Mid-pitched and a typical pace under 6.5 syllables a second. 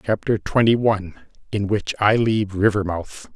No: low, 105 Hz; 4.8 syllables/s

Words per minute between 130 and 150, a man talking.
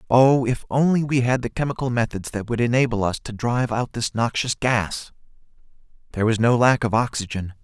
No: average, 190 wpm; male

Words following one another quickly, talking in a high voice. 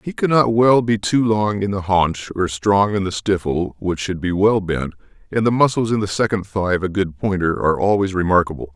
No: fast, 225 wpm; low, 100 Hz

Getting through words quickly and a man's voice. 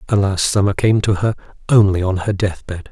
No: average, 185 wpm; male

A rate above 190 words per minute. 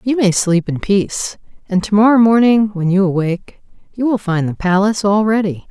Yes: average, 200 wpm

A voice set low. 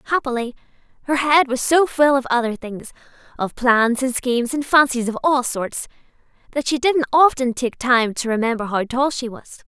No: very high, 255 Hz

